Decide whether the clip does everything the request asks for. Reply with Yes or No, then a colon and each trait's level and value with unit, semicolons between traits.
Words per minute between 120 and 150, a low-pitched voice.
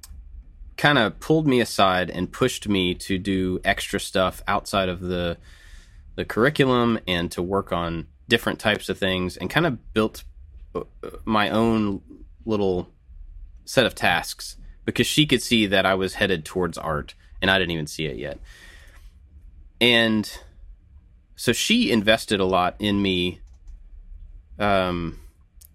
Yes: average, 140 wpm; very low, 90 Hz